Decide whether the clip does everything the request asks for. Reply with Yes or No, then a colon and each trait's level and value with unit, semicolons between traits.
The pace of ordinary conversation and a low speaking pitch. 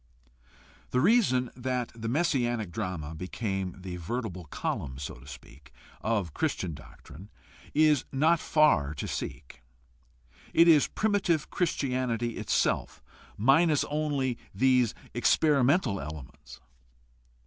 No: slow, 110 wpm; low, 120 Hz